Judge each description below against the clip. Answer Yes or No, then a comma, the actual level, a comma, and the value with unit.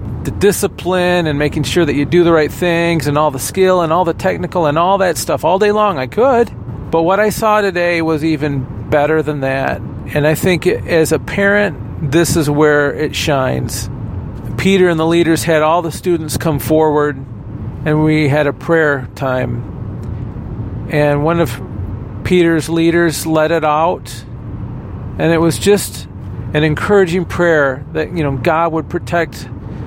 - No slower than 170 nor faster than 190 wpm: Yes, average, 175 wpm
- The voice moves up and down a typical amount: Yes, average, 4.9 semitones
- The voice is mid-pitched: Yes, medium, 155 Hz